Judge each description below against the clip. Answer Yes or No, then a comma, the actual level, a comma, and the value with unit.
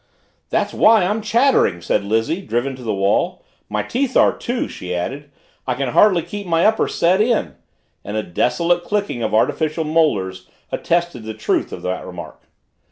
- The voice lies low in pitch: No, medium, 150 Hz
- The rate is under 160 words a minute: No, average, 170 wpm